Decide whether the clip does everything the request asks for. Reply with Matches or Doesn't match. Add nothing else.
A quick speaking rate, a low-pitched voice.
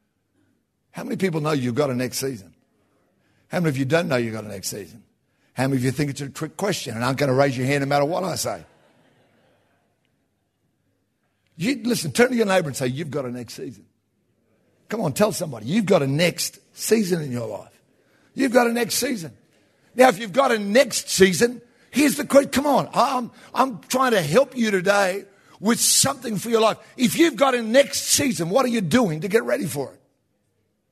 Doesn't match